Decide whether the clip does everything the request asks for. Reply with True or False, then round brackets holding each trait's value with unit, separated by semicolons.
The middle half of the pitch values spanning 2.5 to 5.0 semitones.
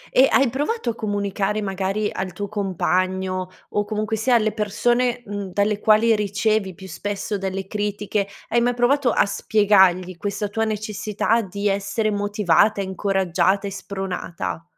False (2.0 semitones)